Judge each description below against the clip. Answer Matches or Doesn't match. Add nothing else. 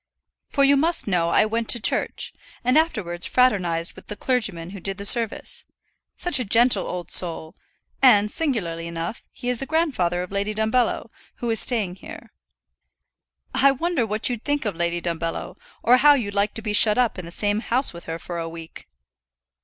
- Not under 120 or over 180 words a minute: Doesn't match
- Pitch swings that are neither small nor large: Doesn't match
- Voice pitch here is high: Matches